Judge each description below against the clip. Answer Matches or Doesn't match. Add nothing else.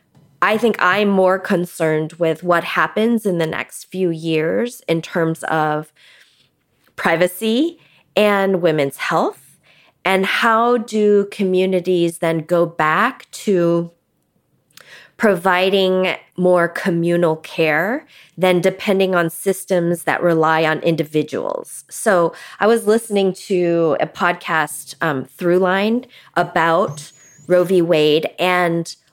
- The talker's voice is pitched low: Doesn't match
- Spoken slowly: Matches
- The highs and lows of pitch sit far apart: Doesn't match